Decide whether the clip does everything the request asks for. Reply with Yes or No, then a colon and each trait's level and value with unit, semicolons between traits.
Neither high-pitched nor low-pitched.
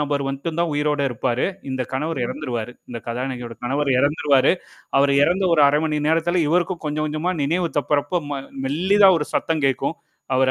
Yes: medium, 145 Hz